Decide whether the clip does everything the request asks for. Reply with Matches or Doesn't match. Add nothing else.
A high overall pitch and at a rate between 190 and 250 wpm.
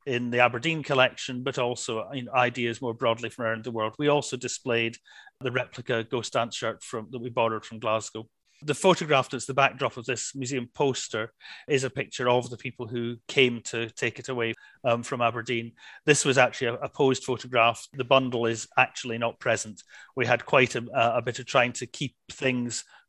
Doesn't match